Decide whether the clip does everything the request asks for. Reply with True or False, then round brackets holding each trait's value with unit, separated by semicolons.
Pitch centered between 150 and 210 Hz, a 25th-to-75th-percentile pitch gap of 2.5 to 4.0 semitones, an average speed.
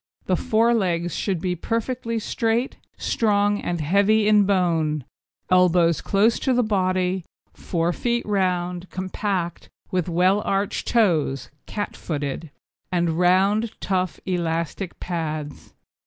False (185 Hz; 3.4 semitones; 120 wpm)